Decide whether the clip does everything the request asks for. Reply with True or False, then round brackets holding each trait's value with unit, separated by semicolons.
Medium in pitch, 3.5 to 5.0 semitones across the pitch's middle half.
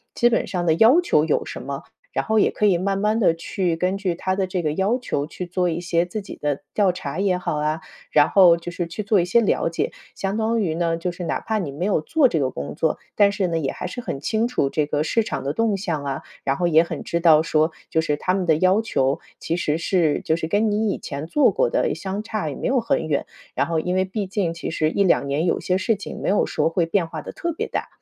True (175 Hz; 4.1 semitones)